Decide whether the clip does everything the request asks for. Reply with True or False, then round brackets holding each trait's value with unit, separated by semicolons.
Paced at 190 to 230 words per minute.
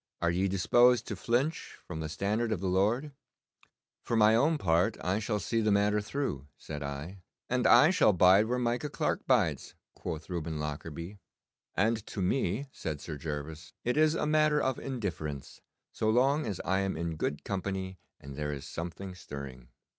False (175 wpm)